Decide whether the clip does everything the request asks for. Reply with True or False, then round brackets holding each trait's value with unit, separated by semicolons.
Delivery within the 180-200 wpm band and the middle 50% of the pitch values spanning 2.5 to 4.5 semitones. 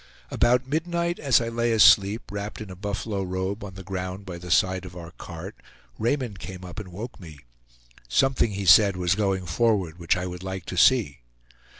True (195 wpm; 3.8 semitones)